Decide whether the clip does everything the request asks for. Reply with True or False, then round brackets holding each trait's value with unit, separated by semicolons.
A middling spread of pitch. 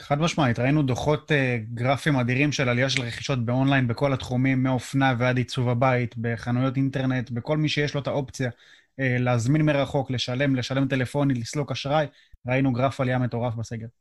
False (2.2 semitones)